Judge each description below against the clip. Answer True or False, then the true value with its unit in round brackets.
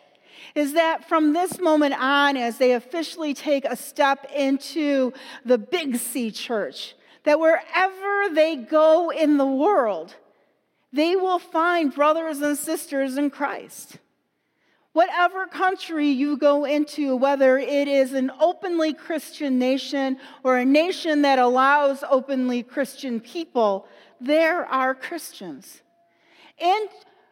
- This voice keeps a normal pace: False (125 wpm)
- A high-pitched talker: True (295 Hz)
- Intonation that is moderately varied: True (3.3 semitones)